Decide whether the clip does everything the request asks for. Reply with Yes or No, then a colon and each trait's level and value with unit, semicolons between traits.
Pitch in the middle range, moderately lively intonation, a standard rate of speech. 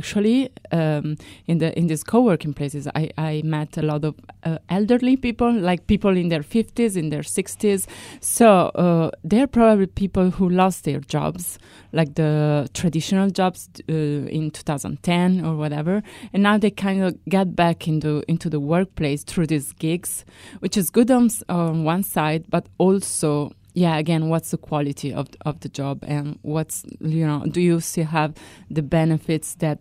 Yes: medium, 165 Hz; average, 3.9 semitones; average, 180 wpm